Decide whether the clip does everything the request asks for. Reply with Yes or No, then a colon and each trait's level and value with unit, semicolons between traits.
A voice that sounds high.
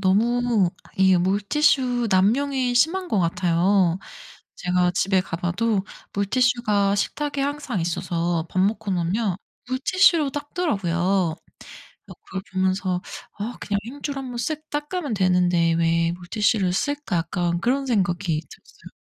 Yes: high, 200 Hz